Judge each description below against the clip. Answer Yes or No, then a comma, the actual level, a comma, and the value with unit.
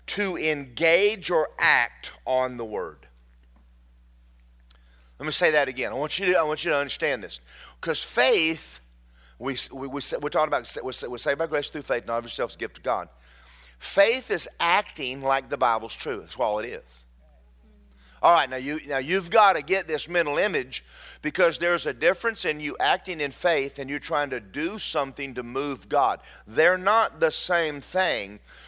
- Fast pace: No, average, 185 wpm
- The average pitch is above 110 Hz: Yes, low, 135 Hz